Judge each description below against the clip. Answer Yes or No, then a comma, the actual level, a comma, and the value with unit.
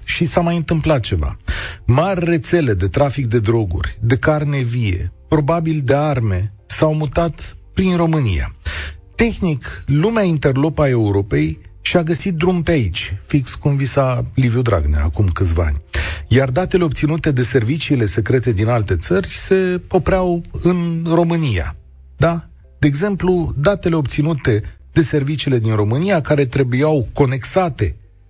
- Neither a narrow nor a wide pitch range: No, wide, 8.8 semitones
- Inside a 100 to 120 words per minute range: No, average, 135 wpm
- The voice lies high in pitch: No, low, 135 Hz